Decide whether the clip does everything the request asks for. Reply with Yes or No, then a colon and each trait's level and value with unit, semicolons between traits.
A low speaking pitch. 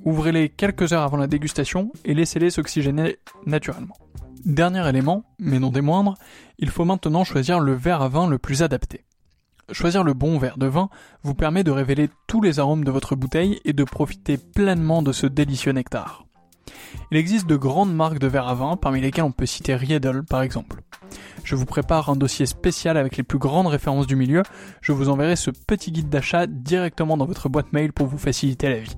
No: medium, 150 Hz